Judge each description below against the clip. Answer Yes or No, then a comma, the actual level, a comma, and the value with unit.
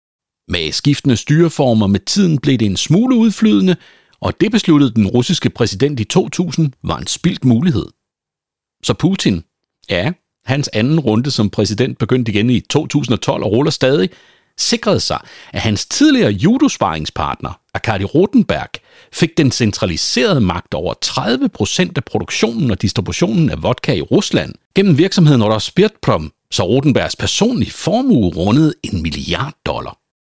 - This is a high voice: No, medium, 140 Hz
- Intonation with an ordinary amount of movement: No, wide, 8.3 semitones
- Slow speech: Yes, slow, 140 wpm